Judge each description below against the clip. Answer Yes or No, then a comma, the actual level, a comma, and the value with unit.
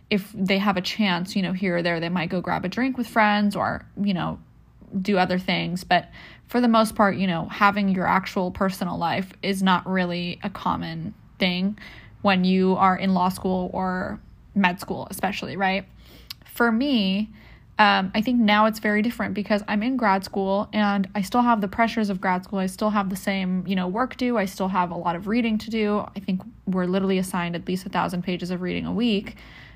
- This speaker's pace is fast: Yes, fast, 220 wpm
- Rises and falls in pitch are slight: Yes, narrow, 2.3 semitones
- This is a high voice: Yes, high, 195 Hz